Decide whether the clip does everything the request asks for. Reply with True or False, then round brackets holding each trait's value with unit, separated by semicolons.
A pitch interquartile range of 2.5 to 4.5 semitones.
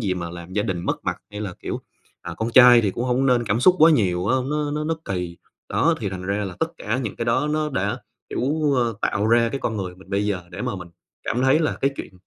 False (5.6 semitones)